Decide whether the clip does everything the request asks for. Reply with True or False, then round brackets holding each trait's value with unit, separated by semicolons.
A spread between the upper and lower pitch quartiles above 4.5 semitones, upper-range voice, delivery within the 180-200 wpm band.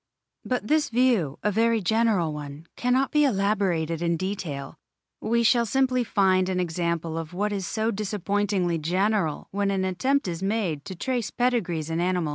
False (5.0 semitones; 195 Hz; 170 wpm)